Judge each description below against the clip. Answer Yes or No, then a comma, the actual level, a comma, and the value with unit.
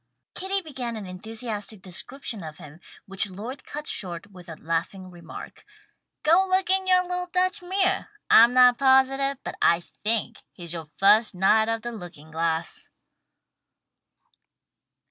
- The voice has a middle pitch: No, high, 225 Hz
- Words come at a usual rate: Yes, average, 145 wpm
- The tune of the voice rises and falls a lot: Yes, wide, 7.4 semitones